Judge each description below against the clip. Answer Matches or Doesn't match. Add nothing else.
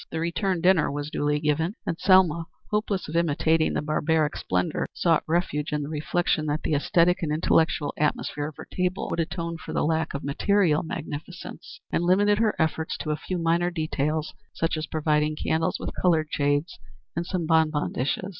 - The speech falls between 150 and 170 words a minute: Doesn't match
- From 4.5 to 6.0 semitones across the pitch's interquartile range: Doesn't match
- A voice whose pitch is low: Doesn't match